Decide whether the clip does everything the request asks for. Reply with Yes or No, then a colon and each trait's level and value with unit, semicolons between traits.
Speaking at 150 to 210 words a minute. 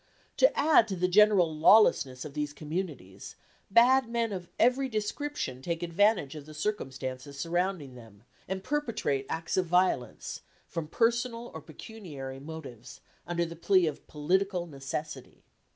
No: average, 140 wpm